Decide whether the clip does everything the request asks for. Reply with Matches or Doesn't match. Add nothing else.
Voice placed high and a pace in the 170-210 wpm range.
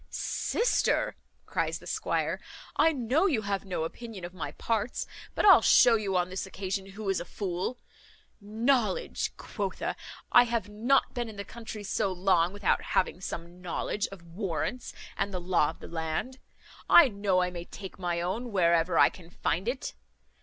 Matches